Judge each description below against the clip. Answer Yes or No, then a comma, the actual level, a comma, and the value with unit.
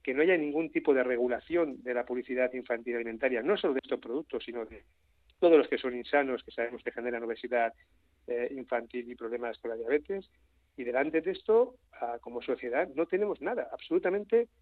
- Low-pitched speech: Yes, low, 125 Hz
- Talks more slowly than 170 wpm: No, average, 185 wpm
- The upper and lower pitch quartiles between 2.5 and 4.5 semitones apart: No, wide, 5.6 semitones